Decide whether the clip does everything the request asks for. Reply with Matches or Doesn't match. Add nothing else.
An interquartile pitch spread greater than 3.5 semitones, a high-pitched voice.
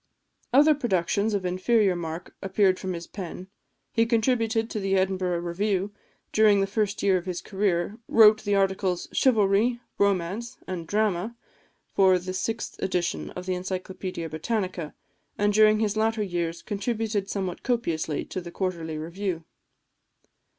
Doesn't match